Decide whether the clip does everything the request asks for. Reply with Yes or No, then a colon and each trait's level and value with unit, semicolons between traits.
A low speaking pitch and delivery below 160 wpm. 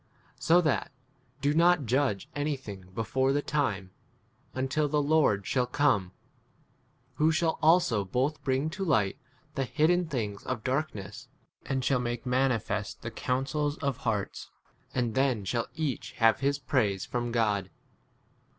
Yes: low, 130 Hz; average, 140 wpm